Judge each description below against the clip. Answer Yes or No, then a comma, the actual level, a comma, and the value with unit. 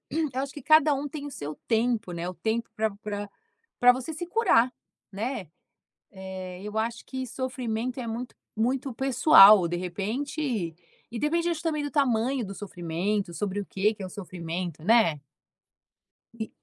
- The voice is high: Yes, high, 225 Hz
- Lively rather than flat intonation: Yes, wide, 5.7 semitones